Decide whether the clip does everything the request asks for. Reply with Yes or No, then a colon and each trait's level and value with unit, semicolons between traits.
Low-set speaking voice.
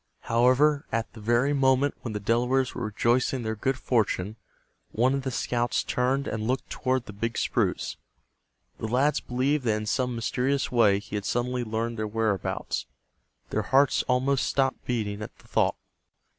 Yes: low, 120 Hz